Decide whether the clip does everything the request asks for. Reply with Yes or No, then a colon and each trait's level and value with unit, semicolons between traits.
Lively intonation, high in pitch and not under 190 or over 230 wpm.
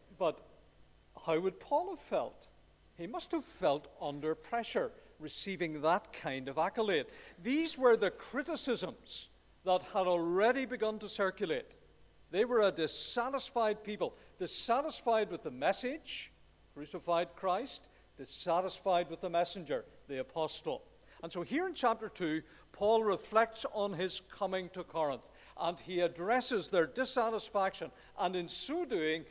No: wide, 6.5 semitones; high, 200 Hz; slow, 135 wpm